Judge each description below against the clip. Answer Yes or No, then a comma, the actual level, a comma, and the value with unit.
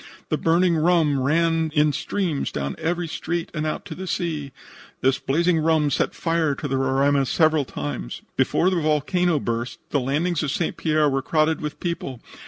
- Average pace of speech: Yes, average, 180 wpm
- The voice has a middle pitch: Yes, medium, 155 Hz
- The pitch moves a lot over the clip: No, average, 3.3 semitones